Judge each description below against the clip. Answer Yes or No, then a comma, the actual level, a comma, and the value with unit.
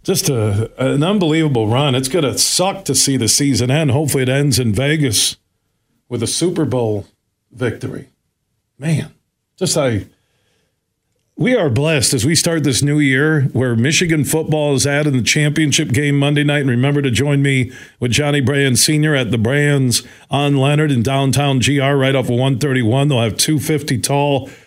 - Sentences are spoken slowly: No, average, 175 wpm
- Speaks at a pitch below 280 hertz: Yes, medium, 140 Hz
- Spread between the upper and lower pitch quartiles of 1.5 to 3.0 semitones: Yes, average, 2.7 semitones